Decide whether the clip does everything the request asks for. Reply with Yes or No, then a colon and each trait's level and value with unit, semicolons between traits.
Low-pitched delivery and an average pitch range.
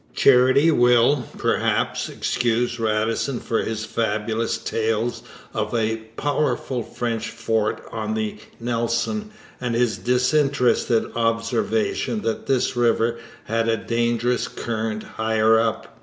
No: low, 115 Hz; narrow, 1.6 semitones